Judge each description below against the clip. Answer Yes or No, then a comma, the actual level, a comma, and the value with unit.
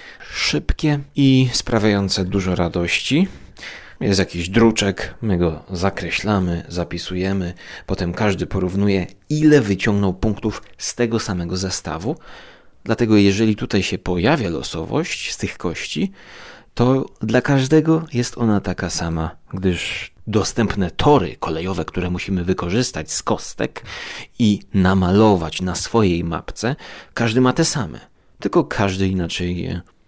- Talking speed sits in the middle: Yes, average, 120 wpm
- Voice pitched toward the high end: No, very low, 95 Hz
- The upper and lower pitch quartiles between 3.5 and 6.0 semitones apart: Yes, average, 4.1 semitones